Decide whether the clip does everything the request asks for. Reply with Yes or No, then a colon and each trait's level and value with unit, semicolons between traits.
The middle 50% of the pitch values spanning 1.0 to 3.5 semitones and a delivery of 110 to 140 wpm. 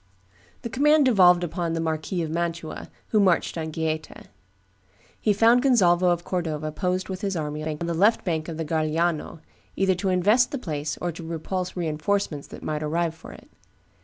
No: average, 3.2 semitones; average, 185 wpm